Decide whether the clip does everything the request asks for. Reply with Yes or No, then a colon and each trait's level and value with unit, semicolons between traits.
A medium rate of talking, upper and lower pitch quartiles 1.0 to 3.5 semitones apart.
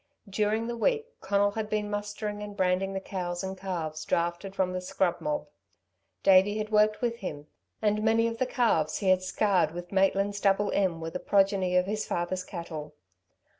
Yes: average, 185 wpm; narrow, 2.5 semitones